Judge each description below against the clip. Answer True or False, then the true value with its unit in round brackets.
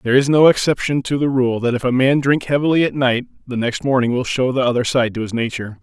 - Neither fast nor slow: False (270 wpm)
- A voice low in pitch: True (130 Hz)